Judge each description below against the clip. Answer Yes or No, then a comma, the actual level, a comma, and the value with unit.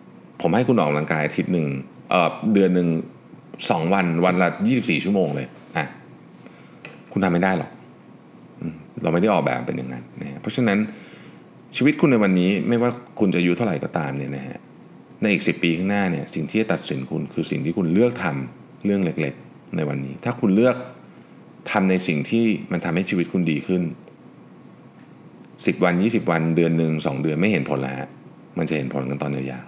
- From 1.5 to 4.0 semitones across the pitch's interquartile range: No, average, 5.1 semitones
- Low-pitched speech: Yes, very low, 85 Hz